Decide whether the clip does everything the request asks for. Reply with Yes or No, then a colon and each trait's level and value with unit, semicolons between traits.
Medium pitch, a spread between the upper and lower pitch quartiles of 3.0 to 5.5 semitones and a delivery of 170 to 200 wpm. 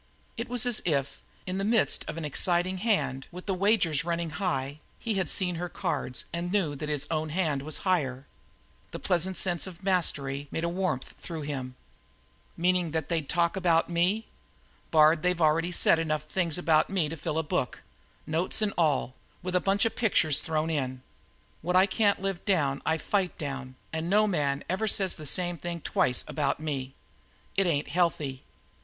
Yes: medium, 170 Hz; average, 3.6 semitones; average, 185 wpm